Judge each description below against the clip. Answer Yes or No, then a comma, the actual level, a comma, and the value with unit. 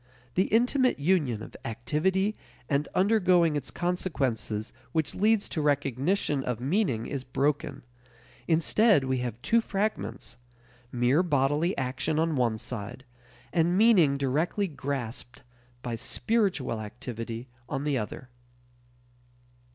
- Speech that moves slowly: Yes, slow, 115 wpm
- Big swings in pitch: Yes, wide, 6.6 semitones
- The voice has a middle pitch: Yes, medium, 145 Hz